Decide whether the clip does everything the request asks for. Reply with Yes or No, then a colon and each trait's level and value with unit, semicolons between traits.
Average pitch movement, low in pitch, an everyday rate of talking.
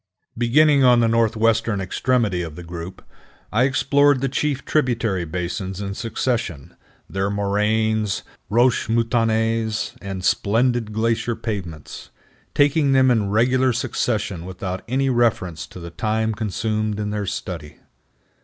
No: average, 3.8 semitones; low, 110 Hz; slow, 125 wpm